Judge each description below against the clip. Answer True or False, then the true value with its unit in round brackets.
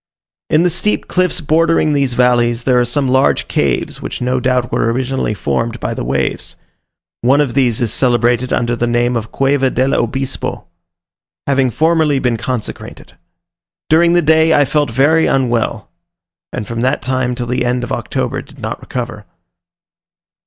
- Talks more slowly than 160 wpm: False (165 wpm)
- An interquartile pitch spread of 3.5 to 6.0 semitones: False (2.9 semitones)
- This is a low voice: True (125 Hz)